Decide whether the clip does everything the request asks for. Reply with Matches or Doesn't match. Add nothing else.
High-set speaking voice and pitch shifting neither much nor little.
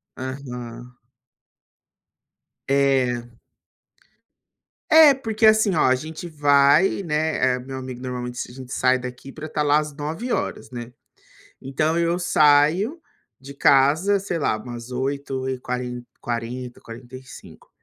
Doesn't match